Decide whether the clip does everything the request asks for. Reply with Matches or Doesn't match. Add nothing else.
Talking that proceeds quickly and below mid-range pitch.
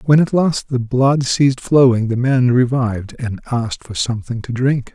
Doesn't match